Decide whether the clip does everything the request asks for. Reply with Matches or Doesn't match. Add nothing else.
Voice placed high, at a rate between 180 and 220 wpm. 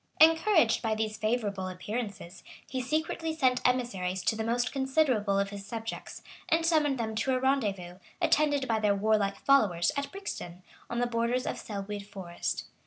Doesn't match